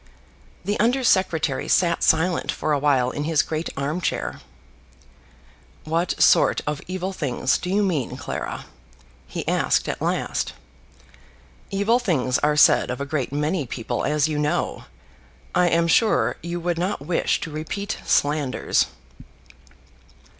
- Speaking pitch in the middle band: Yes, medium, 160 Hz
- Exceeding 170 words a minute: No, average, 140 wpm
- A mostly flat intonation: No, average, 3.7 semitones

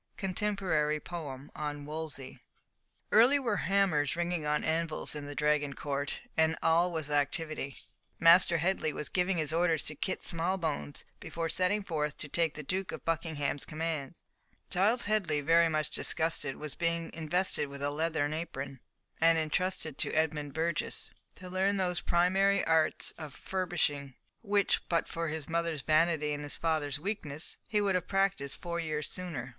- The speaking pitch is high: No, medium, 160 Hz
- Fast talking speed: No, average, 160 wpm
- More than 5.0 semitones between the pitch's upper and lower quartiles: No, average, 3.2 semitones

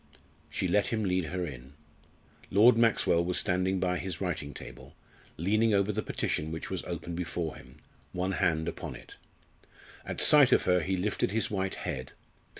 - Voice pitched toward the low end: Yes, very low, 90 Hz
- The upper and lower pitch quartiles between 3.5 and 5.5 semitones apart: No, average, 2.8 semitones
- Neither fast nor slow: Yes, average, 170 wpm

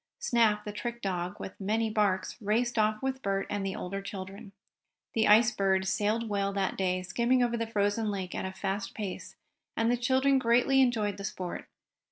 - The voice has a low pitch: No, high, 210 Hz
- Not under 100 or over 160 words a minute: No, average, 190 wpm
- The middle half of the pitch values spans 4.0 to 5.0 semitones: No, average, 3.2 semitones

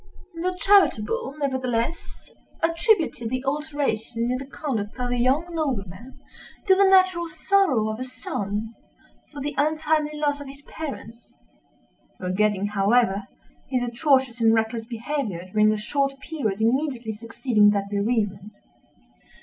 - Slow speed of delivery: Yes, slow, 125 wpm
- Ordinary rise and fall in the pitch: No, wide, 5.8 semitones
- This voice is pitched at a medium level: No, high, 245 Hz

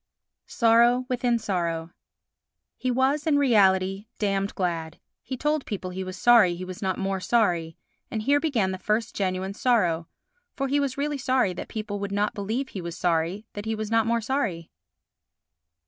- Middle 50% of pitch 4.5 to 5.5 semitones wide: Yes, average, 4.8 semitones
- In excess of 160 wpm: Yes, average, 175 wpm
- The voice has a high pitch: Yes, high, 210 Hz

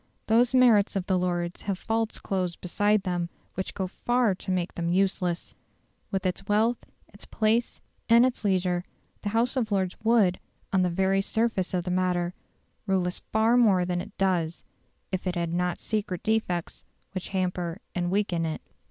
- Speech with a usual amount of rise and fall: Yes, average, 3.3 semitones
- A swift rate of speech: No, average, 175 wpm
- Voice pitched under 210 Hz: Yes, high, 190 Hz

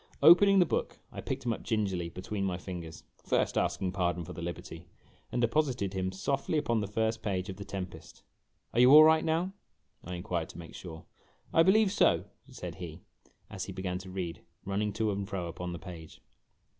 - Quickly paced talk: Yes, fast, 210 wpm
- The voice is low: Yes, very low, 95 Hz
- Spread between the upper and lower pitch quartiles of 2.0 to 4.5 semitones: No, average, 4.9 semitones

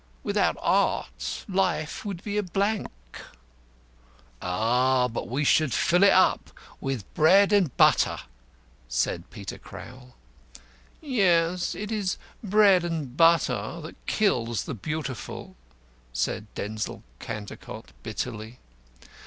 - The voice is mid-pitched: Yes, medium, 155 Hz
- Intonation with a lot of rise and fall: Yes, wide, 8.6 semitones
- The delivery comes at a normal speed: No, slow, 110 wpm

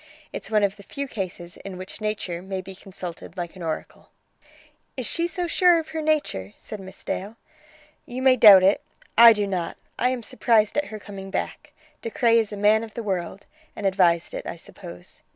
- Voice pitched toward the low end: No, high, 210 Hz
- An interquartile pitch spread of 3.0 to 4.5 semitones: Yes, average, 4.2 semitones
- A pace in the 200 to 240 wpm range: Yes, fast, 205 wpm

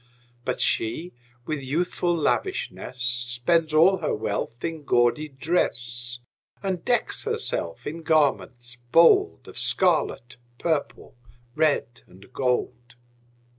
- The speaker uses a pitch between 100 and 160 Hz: Yes, medium, 140 Hz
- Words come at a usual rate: No, slow, 105 wpm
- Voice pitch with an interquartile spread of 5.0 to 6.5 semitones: Yes, wide, 5.4 semitones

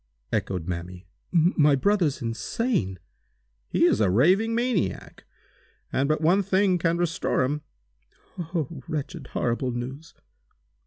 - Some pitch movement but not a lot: No, wide, 7.0 semitones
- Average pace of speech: No, slow, 115 wpm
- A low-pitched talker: No, medium, 155 Hz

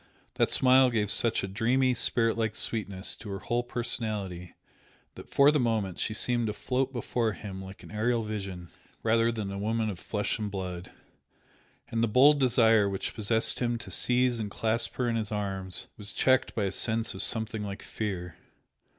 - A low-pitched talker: Yes, low, 110 Hz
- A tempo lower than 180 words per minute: No, average, 185 wpm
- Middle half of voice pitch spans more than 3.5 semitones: No, average, 3.0 semitones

